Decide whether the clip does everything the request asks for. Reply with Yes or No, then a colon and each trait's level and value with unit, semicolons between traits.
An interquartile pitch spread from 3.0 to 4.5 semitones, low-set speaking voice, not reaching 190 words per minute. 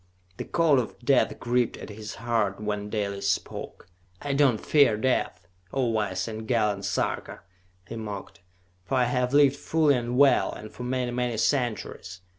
Yes: average, 3.6 semitones; low, 120 Hz; average, 170 wpm